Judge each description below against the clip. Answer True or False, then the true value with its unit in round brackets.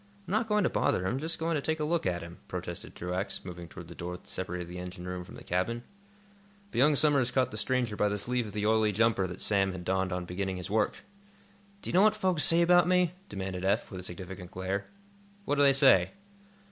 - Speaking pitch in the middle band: False (105 Hz)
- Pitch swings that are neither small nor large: False (7.8 semitones)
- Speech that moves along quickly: True (240 wpm)